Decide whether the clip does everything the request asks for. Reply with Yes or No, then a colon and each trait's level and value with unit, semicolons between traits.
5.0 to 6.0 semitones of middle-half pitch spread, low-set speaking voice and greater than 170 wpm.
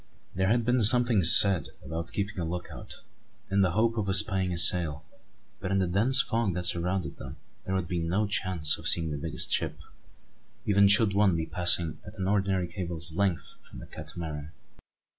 No: average, 3.1 semitones; very low, 95 Hz; average, 190 wpm